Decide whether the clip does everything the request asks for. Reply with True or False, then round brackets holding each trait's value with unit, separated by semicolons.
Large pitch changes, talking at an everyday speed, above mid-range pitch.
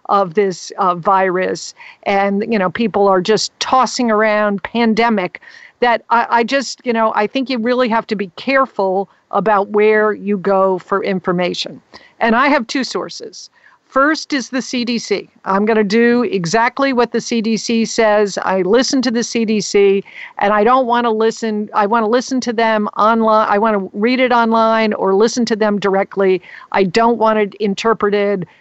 False (2.8 semitones; 180 wpm; 220 Hz)